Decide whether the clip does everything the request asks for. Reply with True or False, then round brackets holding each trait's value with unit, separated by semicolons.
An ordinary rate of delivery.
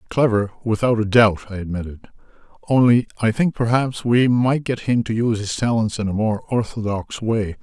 True (180 wpm)